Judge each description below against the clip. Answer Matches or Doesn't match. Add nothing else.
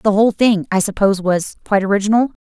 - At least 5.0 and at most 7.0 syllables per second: Matches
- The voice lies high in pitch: Matches